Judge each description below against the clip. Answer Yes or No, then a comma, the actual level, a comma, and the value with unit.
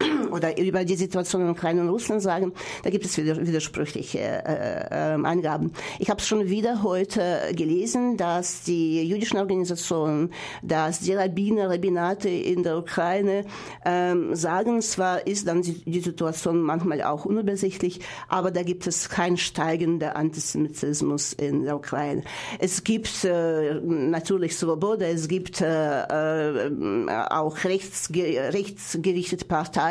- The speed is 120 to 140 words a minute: Yes, average, 130 wpm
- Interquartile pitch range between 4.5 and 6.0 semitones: No, average, 2.8 semitones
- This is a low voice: No, medium, 175 Hz